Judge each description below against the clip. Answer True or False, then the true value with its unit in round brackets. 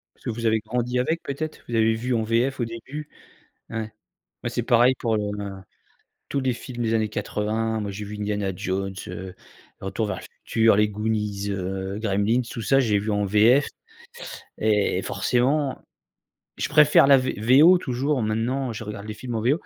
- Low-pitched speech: True (110 Hz)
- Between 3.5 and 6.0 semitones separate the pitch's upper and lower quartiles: False (3.1 semitones)